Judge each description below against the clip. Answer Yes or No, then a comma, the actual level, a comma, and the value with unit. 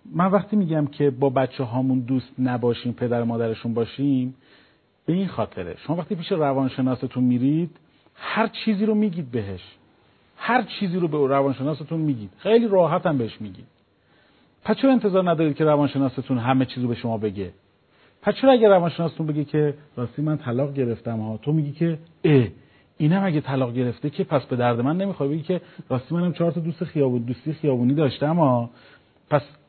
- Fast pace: Yes, fast, 170 wpm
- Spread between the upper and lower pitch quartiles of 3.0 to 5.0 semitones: No, wide, 5.4 semitones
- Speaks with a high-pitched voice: No, medium, 140 Hz